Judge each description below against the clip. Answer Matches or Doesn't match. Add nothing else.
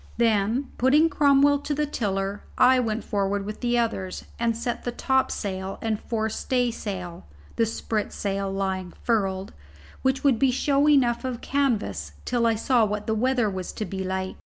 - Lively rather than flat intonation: Doesn't match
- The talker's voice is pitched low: Doesn't match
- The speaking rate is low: Doesn't match